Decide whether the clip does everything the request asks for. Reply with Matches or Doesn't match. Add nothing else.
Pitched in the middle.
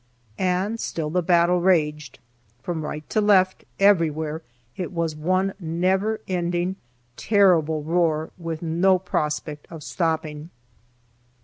Matches